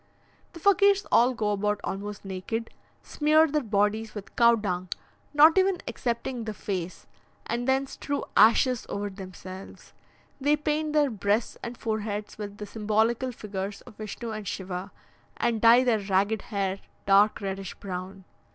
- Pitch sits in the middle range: No, high, 215 Hz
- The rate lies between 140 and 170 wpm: Yes, average, 150 wpm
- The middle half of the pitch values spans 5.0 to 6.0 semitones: No, average, 4.0 semitones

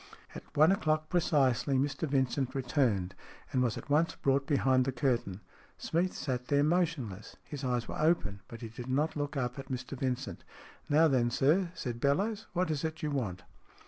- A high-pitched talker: No, low, 135 Hz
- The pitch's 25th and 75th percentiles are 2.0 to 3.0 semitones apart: No, average, 3.8 semitones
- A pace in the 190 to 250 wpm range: No, average, 180 wpm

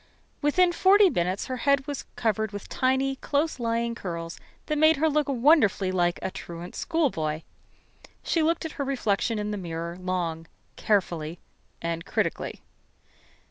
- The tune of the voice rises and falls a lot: Yes, wide, 8.6 semitones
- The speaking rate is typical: Yes, average, 145 wpm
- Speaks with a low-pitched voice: No, high, 230 Hz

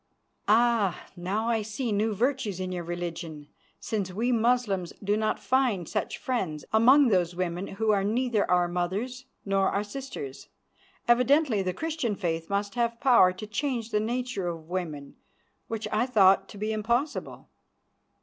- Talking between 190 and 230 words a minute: No, average, 155 wpm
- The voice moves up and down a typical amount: Yes, average, 4.6 semitones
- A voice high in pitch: Yes, high, 210 Hz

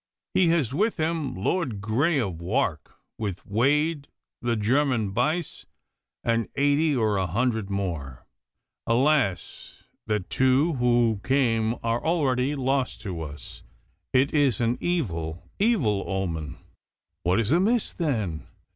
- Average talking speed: No, slow, 125 wpm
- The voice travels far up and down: Yes, wide, 6.5 semitones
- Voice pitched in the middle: No, low, 120 Hz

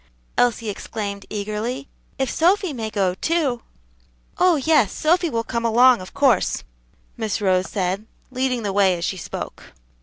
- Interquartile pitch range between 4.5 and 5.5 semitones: Yes, average, 4.9 semitones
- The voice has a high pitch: Yes, high, 230 Hz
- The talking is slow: No, average, 150 wpm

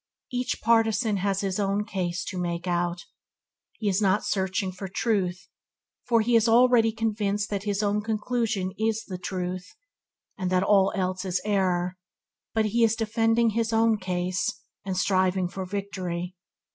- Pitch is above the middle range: Yes, high, 200 Hz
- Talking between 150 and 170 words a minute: Yes, average, 160 wpm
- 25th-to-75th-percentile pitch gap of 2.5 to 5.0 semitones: Yes, average, 3.2 semitones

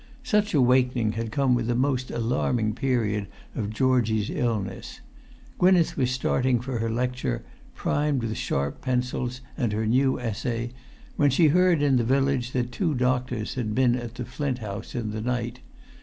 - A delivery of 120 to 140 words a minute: No, average, 165 wpm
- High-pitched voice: No, low, 125 Hz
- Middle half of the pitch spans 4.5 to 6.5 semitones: No, narrow, 2.5 semitones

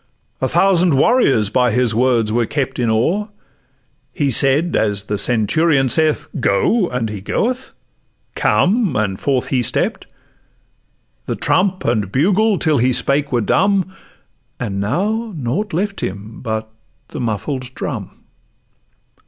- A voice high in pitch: No, low, 130 Hz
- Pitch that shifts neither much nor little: No, wide, 8.4 semitones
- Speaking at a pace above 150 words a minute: No, slow, 135 wpm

